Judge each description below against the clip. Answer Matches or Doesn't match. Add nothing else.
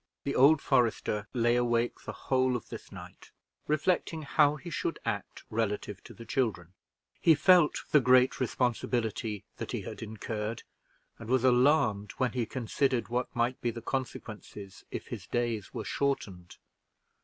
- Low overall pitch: Matches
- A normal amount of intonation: Matches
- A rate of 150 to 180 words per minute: Matches